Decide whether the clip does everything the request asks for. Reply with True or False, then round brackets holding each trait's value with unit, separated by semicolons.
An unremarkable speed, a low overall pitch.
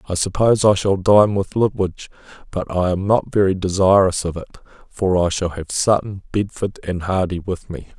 True (190 wpm; 95 Hz)